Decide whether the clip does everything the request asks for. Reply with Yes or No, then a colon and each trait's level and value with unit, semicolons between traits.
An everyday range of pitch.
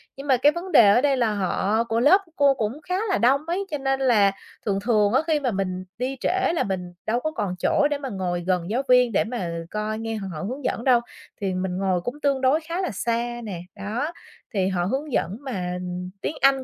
No: wide, 5.9 semitones